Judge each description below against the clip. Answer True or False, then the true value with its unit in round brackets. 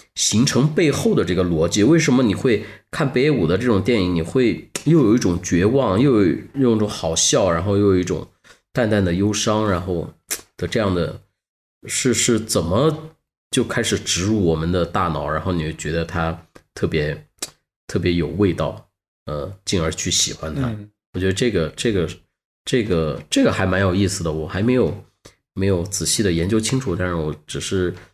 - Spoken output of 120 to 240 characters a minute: False (265 characters per minute)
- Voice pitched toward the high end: False (95 Hz)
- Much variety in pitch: False (4.5 semitones)